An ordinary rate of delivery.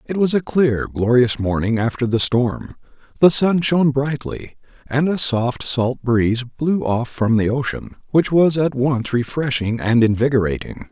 Yes: average, 165 wpm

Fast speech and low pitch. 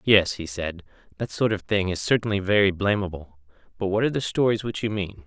Yes: fast, 215 wpm; low, 100 Hz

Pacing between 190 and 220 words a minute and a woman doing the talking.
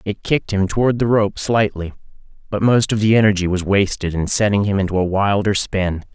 No: fast, 205 wpm; male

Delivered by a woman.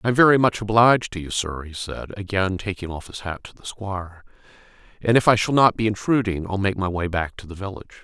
No: male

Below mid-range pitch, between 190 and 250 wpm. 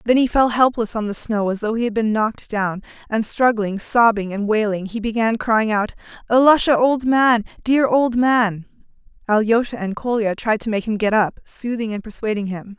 No: high, 220 Hz; average, 195 wpm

